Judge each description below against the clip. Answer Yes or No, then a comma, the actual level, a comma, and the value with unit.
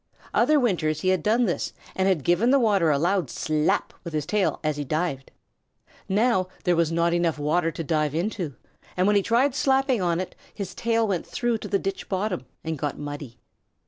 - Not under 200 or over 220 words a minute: Yes, fast, 205 wpm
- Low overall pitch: No, medium, 180 Hz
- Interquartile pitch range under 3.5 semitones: No, average, 5.2 semitones